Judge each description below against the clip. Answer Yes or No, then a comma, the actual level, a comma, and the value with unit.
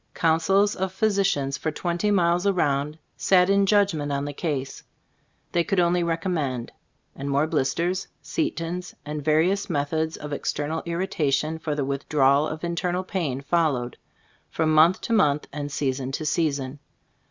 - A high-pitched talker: No, medium, 160 Hz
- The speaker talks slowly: No, average, 145 wpm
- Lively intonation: No, average, 3.9 semitones